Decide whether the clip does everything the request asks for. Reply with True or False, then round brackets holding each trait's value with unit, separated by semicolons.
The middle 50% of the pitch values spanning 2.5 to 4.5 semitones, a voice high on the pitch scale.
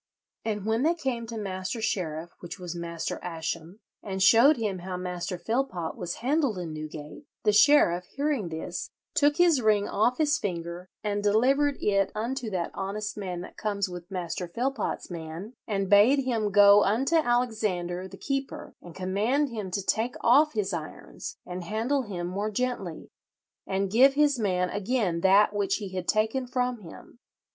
False (5.3 semitones; 205 Hz)